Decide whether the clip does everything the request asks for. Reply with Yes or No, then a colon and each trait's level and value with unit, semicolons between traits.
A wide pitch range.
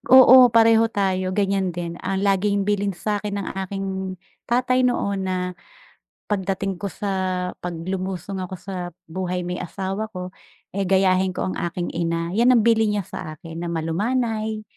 No: narrow, 2.4 semitones